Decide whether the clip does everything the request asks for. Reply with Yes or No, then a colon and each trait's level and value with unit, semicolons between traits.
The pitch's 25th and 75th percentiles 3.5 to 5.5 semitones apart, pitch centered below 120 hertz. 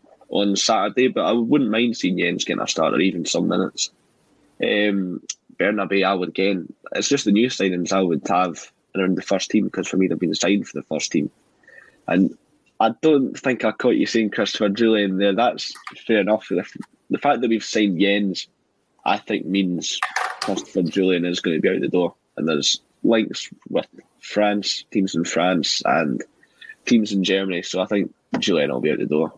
No: narrow, 2.4 semitones; low, 100 Hz